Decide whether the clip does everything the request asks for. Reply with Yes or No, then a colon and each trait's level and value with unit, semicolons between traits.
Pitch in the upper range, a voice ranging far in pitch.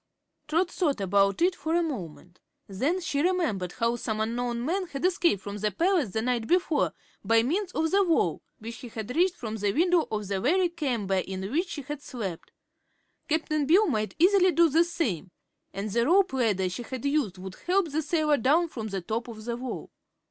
Yes: very high, 260 Hz; wide, 7.9 semitones